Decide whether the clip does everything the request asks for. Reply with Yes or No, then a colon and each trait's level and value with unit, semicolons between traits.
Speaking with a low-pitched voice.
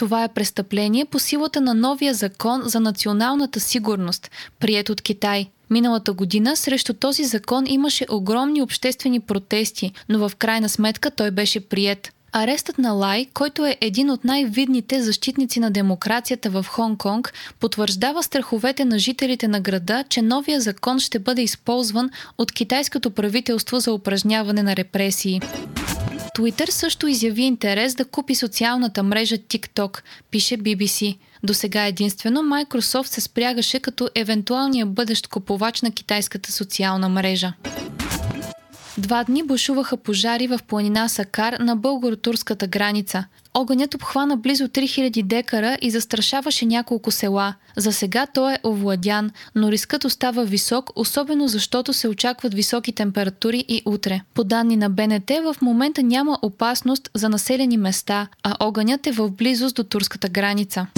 No: high, 230 Hz